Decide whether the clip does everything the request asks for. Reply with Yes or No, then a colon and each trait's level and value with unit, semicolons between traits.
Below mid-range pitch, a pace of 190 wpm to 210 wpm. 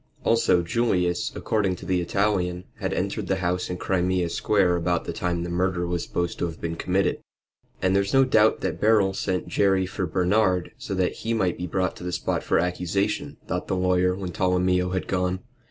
Yes: very low, 90 Hz; average, 200 wpm